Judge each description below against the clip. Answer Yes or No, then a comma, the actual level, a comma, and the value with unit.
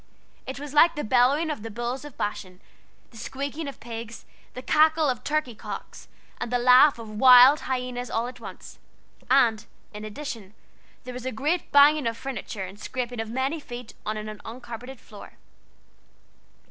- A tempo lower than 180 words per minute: Yes, average, 170 wpm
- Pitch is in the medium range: No, very high, 250 Hz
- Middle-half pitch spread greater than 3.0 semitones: Yes, average, 3.6 semitones